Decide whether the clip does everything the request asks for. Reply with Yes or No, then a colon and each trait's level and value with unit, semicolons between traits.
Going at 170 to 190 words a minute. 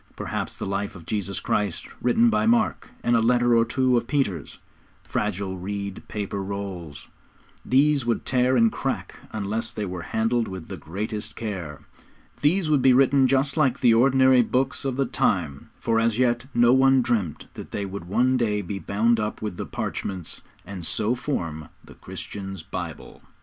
Yes: average, 175 wpm